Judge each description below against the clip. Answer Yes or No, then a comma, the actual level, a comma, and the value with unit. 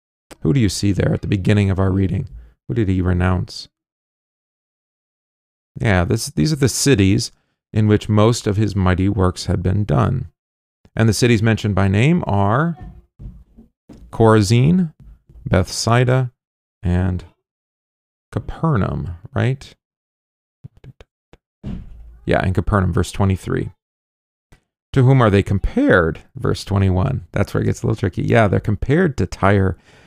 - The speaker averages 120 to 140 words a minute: Yes, slow, 135 wpm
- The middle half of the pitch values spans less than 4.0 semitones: No, average, 4.4 semitones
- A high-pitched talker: No, low, 100 Hz